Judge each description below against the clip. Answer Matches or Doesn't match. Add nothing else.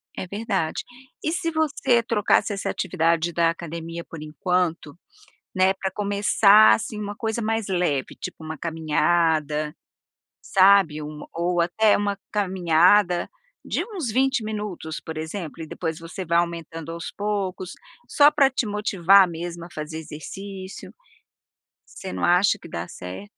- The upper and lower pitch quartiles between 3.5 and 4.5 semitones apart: Matches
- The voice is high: Doesn't match